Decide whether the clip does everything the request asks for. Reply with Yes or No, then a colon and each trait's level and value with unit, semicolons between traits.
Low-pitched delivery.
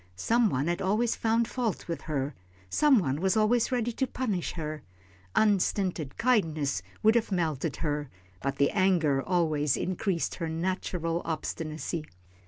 No: medium, 175 Hz